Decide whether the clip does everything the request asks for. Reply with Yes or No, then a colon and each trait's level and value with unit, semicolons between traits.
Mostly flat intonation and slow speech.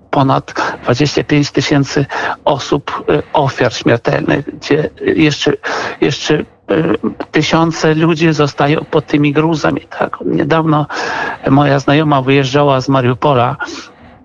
Yes: narrow, 2.0 semitones; slow, 95 wpm